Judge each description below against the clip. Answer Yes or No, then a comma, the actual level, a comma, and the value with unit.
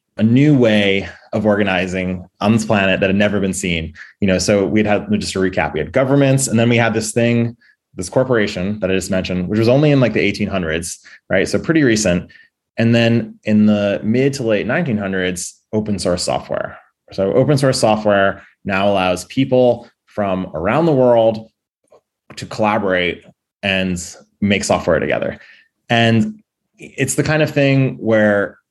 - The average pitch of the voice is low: Yes, low, 105 Hz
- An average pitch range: Yes, average, 3.7 semitones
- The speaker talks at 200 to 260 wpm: No, average, 175 wpm